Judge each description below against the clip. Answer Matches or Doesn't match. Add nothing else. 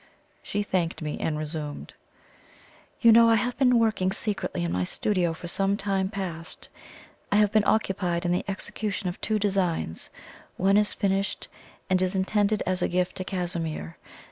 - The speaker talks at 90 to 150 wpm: Doesn't match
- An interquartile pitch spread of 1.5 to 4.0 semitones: Matches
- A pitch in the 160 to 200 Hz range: Matches